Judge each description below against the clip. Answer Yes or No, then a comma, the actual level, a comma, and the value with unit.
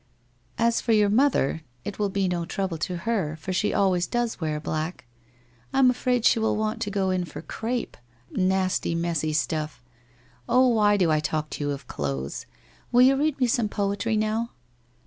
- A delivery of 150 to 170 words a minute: No, average, 195 wpm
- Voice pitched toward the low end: No, high, 195 Hz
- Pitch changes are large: Yes, wide, 6.1 semitones